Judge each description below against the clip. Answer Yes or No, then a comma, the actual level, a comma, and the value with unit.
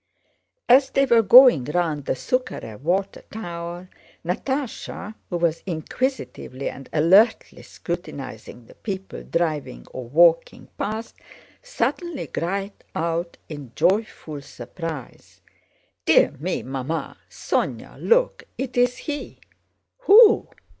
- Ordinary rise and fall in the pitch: No, wide, 7.8 semitones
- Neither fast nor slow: No, slow, 105 wpm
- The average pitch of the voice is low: No, medium, 175 Hz